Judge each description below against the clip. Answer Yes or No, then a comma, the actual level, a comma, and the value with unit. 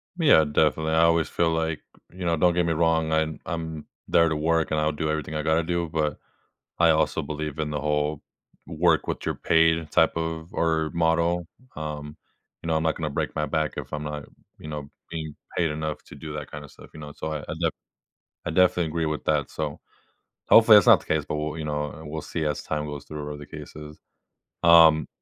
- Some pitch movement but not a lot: No, narrow, 1.5 semitones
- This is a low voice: Yes, very low, 80 Hz